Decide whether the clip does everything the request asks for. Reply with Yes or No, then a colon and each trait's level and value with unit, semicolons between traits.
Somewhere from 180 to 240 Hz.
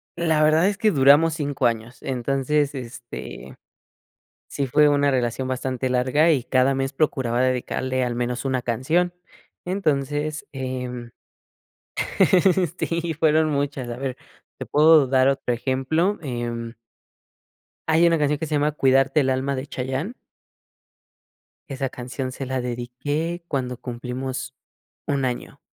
No: low, 135 Hz